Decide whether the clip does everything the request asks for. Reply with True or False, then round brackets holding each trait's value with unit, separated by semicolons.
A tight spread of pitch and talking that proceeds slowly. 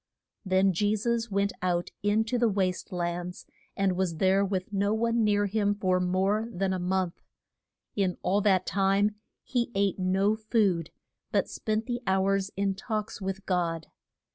False (2.2 semitones; 165 wpm)